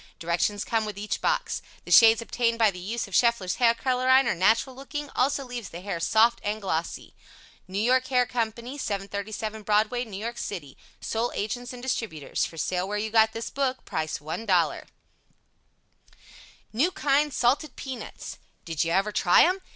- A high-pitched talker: Yes, high, 225 Hz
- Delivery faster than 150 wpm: Yes, average, 170 wpm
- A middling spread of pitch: Yes, average, 3.9 semitones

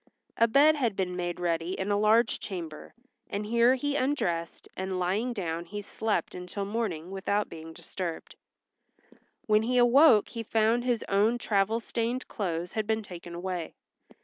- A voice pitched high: Yes, high, 205 Hz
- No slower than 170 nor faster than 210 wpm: No, average, 160 wpm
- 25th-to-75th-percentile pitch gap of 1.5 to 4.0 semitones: No, average, 4.5 semitones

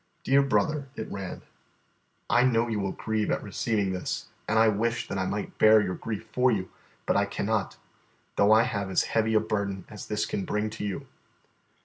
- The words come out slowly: No, average, 200 wpm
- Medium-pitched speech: No, low, 110 Hz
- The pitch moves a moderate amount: No, narrow, 2.1 semitones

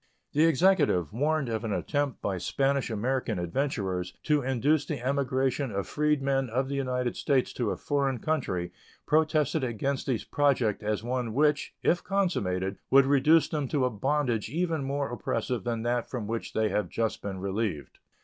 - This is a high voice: No, low, 130 Hz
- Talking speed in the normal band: Yes, average, 170 wpm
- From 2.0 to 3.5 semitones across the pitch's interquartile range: No, average, 4.6 semitones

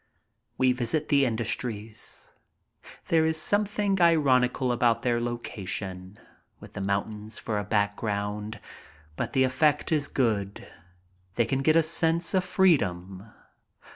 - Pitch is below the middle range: Yes, low, 120 Hz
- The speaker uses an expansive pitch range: Yes, wide, 7.0 semitones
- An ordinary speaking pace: No, slow, 125 wpm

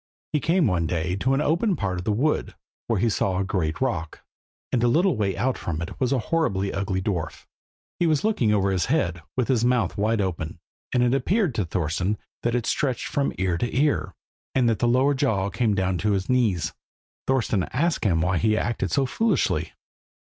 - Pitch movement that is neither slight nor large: No, wide, 6.0 semitones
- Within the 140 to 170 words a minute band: No, fast, 205 wpm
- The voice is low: Yes, low, 110 Hz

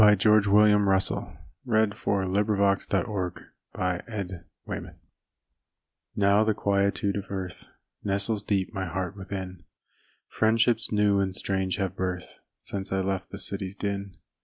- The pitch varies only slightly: Yes, narrow, 1.5 semitones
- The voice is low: Yes, low, 100 Hz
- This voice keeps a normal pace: No, slow, 115 wpm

